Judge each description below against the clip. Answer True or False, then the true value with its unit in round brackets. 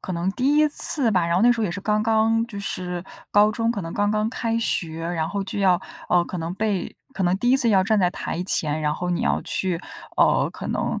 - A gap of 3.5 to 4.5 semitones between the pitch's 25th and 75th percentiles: True (4.1 semitones)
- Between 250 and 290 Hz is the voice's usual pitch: False (195 Hz)